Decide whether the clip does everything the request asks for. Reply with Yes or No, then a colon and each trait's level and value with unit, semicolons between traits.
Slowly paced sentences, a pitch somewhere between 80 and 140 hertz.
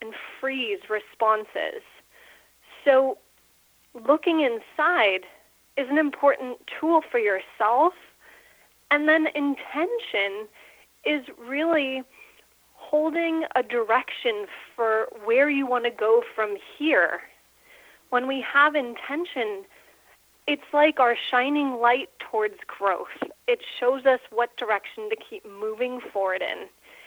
No: slow, 110 wpm; very high, 275 Hz